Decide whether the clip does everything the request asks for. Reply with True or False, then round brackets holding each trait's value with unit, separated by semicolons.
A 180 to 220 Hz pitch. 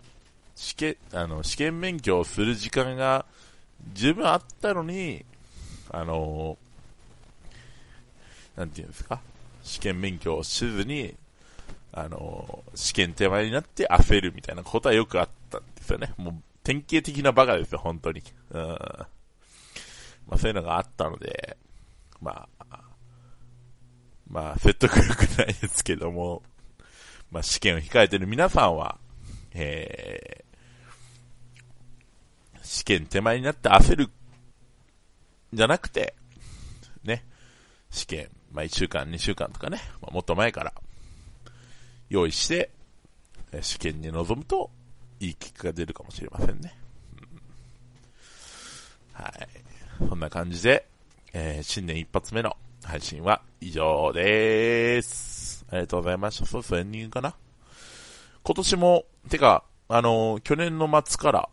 False (110 Hz)